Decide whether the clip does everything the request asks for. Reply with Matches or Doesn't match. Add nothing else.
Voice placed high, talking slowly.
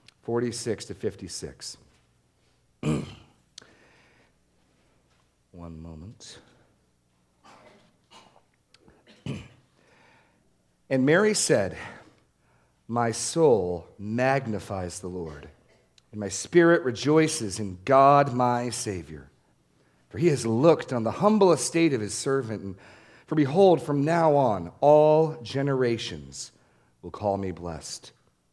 Doesn't match